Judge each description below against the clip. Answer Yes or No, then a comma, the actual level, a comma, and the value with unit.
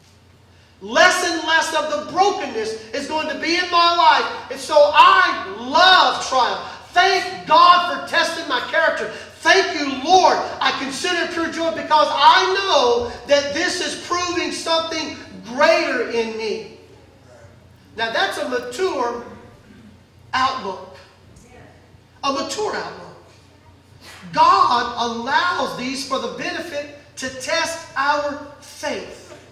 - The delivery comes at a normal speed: No, slow, 125 wpm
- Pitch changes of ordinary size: Yes, average, 4.5 semitones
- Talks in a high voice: Yes, very high, 310 Hz